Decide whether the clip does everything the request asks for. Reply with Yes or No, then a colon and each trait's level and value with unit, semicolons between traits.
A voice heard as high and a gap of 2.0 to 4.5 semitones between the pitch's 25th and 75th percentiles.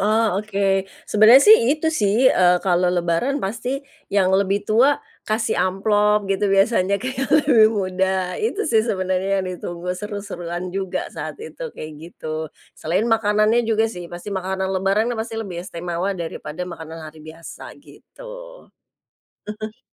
Yes: high, 195 Hz; average, 3.3 semitones